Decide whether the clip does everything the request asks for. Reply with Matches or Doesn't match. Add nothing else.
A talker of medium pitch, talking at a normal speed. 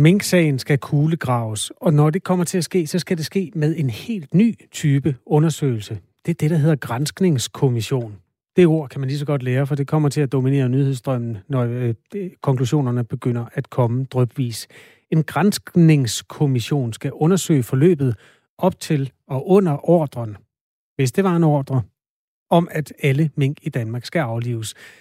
Matches